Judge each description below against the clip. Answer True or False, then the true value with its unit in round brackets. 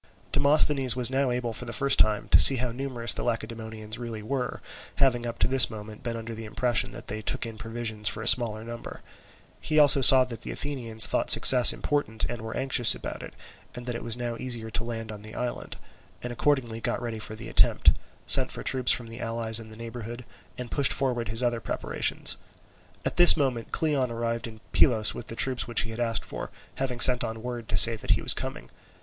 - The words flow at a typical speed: False (220 wpm)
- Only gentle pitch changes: True (2.0 semitones)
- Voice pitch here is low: True (120 Hz)